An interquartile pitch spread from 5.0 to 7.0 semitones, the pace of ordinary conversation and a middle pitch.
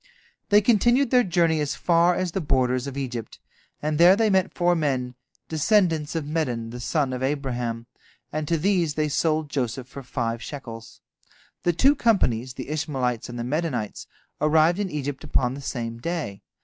Yes: wide, 5.4 semitones; average, 175 wpm; medium, 150 Hz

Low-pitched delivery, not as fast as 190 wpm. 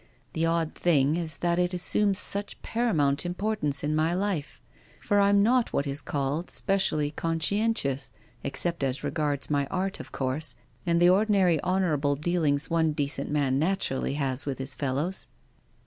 No: medium, 160 Hz; average, 155 wpm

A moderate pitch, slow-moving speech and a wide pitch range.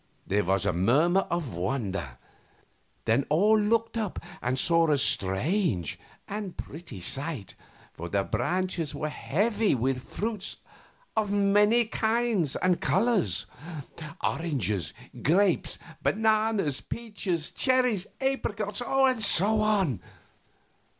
Yes: medium, 180 Hz; slow, 110 wpm; wide, 8.4 semitones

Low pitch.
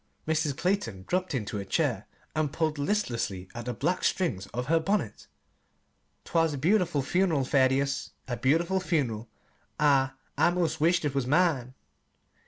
No: medium, 150 Hz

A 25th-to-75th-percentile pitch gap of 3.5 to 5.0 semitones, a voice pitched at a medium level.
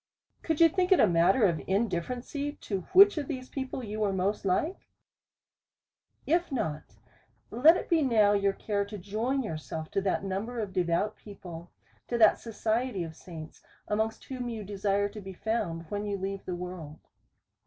No: average, 4.6 semitones; high, 205 Hz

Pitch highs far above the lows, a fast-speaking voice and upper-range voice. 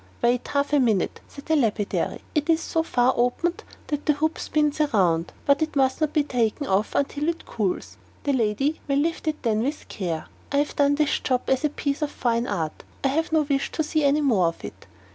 No: average, 4.4 semitones; fast, 220 wpm; very high, 280 Hz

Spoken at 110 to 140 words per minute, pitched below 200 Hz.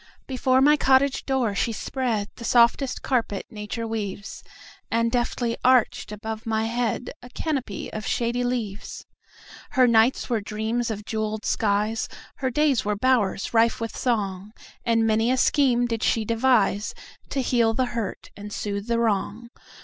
No: slow, 135 wpm; high, 230 Hz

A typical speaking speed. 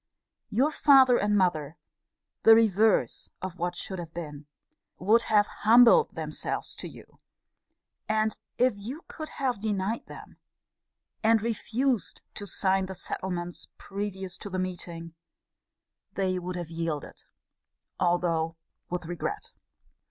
No: slow, 120 wpm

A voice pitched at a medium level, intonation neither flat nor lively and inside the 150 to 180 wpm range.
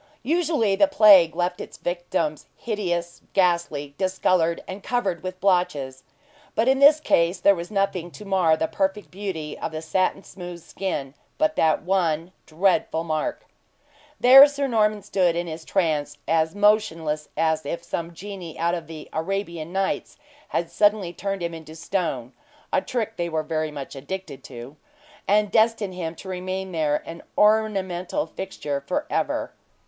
Yes: medium, 180 Hz; average, 3.8 semitones; average, 155 wpm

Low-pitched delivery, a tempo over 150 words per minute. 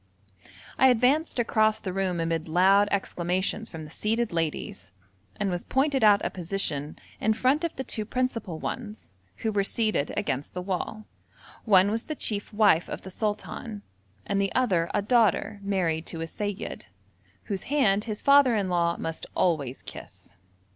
No: high, 200 Hz; average, 165 wpm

